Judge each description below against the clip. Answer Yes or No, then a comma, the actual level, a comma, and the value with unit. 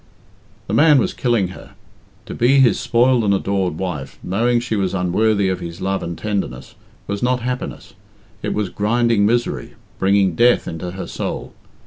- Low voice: Yes, low, 100 Hz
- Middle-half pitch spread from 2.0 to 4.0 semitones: No, average, 4.4 semitones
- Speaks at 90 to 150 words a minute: No, average, 165 wpm